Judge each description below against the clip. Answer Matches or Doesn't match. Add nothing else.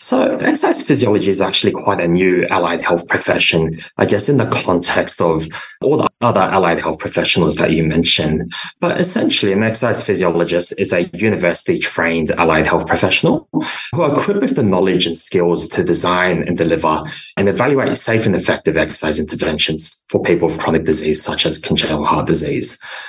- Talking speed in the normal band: Matches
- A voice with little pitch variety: Doesn't match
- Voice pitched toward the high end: Doesn't match